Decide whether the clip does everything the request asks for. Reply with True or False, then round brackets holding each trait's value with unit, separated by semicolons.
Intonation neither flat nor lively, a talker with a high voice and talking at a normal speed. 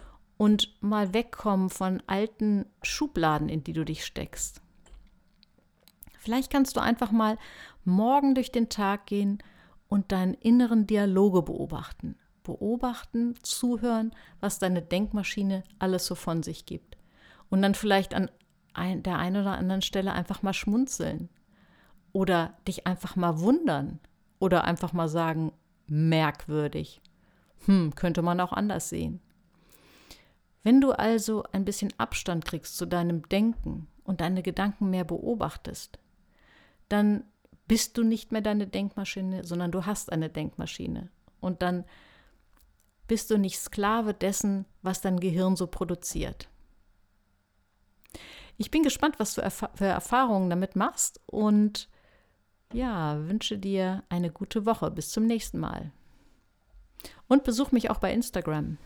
True (3.6 semitones; 195 Hz; 135 wpm)